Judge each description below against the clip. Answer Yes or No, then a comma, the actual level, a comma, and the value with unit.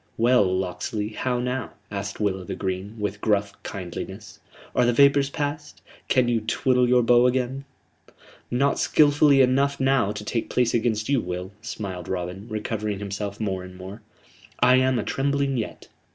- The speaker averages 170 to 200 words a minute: No, average, 160 wpm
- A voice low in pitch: Yes, low, 115 Hz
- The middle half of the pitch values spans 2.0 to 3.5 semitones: No, average, 4.4 semitones